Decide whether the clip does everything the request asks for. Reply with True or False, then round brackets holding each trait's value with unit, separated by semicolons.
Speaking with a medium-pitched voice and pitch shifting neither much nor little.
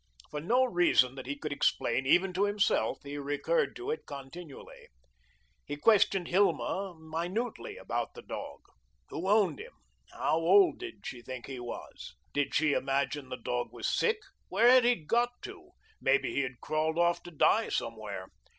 False (170 Hz; 8.1 semitones)